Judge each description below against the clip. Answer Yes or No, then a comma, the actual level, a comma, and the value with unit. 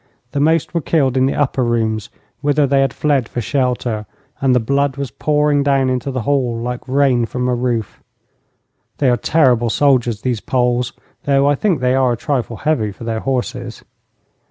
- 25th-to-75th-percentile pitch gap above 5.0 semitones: No, average, 2.8 semitones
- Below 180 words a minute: No, average, 185 wpm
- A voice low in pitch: Yes, low, 130 Hz